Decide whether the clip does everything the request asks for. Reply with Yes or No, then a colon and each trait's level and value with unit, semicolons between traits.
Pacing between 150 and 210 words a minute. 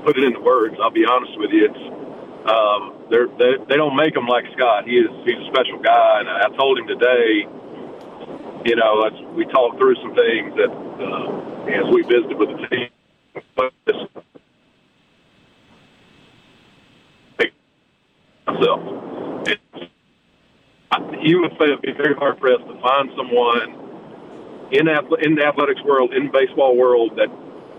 No: average, 140 wpm